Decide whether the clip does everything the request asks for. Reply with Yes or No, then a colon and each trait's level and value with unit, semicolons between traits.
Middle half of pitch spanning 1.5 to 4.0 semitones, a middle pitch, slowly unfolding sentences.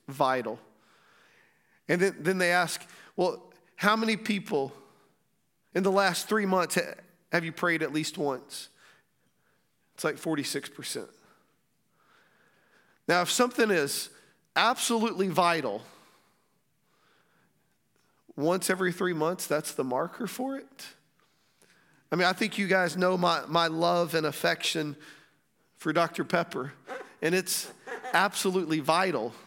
Yes: average, 2.9 semitones; medium, 180 Hz; slow, 120 wpm